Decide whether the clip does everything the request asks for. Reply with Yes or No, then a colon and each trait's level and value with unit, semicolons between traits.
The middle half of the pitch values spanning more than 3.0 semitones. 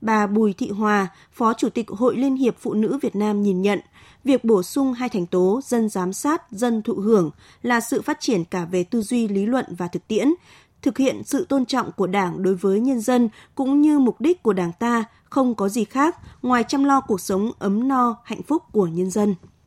Yes: average, 4.6 semitones